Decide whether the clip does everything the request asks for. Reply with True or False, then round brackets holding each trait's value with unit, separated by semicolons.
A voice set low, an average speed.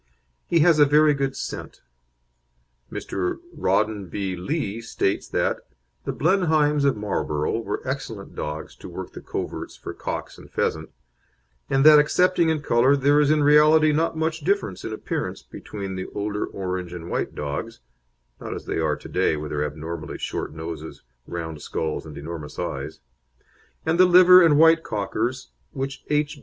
True (120 Hz; 165 wpm)